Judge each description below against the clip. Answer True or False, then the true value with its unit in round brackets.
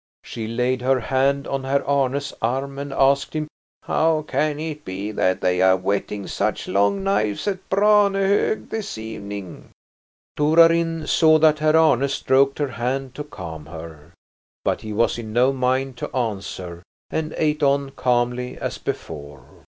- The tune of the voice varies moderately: False (6.1 semitones)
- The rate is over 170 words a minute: False (155 wpm)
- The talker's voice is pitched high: False (135 Hz)